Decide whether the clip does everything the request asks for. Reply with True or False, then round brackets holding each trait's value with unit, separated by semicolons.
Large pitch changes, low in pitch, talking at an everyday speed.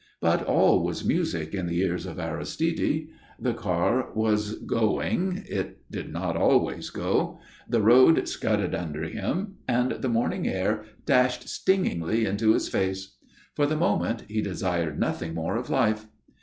True (5.8 semitones; 110 Hz; 150 wpm)